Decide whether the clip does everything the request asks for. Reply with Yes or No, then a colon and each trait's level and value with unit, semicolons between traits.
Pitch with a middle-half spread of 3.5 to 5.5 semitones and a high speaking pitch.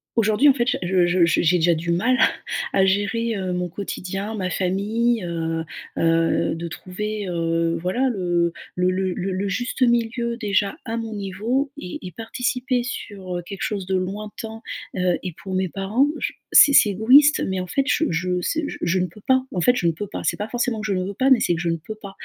Yes: average, 4.2 semitones; high, 195 Hz